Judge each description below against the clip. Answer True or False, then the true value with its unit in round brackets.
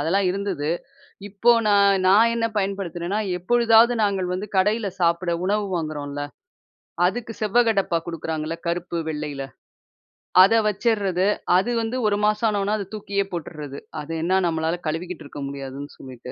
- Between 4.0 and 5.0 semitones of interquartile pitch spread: True (4.5 semitones)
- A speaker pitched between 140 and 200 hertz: True (185 Hz)